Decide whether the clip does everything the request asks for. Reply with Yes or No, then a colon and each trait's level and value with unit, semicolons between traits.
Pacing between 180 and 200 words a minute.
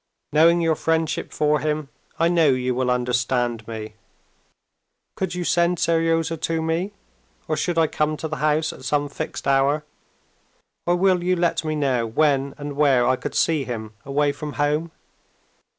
No: average, 165 wpm